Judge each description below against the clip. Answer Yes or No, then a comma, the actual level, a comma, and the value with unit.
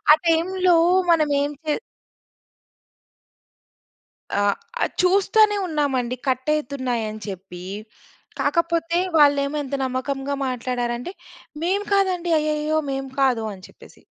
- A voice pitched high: Yes, very high, 285 Hz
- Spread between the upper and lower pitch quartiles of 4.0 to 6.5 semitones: Yes, average, 4.9 semitones